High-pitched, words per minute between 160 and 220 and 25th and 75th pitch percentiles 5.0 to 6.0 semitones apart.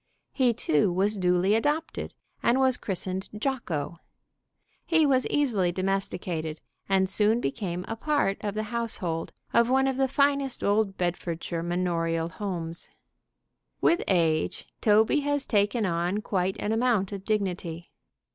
No: high, 200 Hz; slow, 135 wpm; average, 5.3 semitones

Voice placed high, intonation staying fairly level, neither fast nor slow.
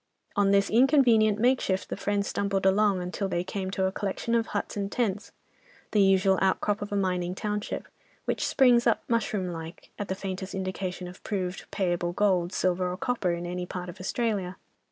Yes: high, 195 Hz; narrow, 2.3 semitones; average, 185 wpm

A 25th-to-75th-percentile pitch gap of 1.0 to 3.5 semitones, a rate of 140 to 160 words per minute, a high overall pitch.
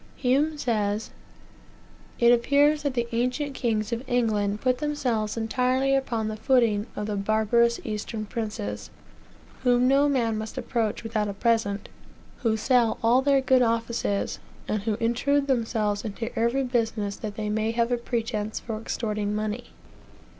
Yes: average, 2.8 semitones; average, 150 wpm; high, 230 Hz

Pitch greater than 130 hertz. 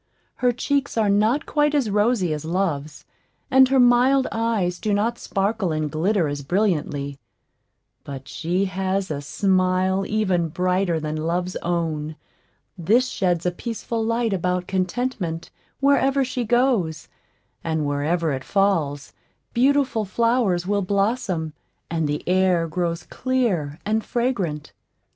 Yes: high, 190 Hz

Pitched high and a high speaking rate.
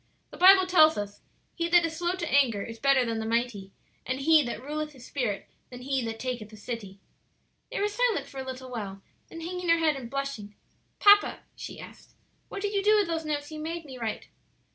Yes: very high, 275 Hz; fast, 220 wpm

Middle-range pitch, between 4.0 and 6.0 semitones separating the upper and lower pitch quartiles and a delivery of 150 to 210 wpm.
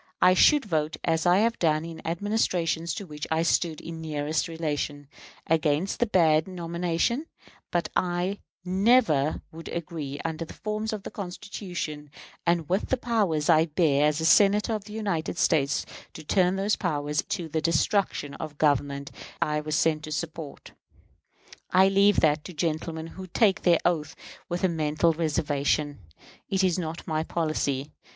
No: medium, 165 Hz; average, 3.3 semitones; average, 165 wpm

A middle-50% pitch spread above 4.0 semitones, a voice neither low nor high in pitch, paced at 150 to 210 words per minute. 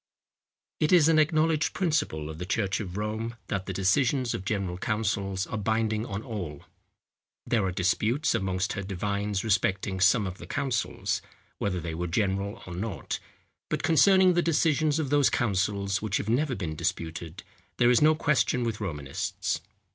No: wide, 5.4 semitones; low, 105 Hz; average, 165 wpm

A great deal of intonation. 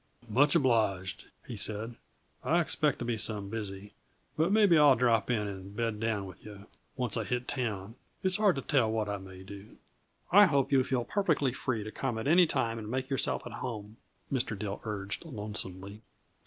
No: average, 4.6 semitones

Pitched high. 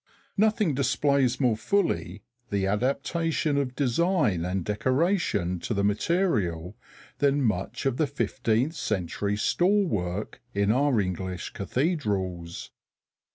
No: low, 125 Hz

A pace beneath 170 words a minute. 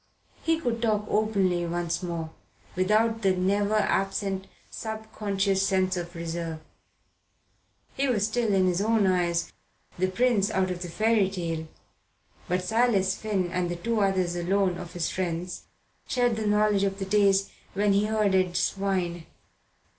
Yes: average, 145 wpm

